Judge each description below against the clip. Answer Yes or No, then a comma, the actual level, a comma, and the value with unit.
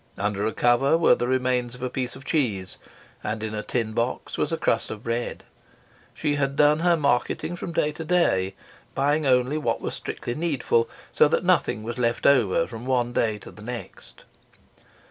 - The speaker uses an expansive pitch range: No, average, 4.0 semitones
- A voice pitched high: No, low, 125 Hz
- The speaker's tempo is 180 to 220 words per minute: Yes, average, 190 wpm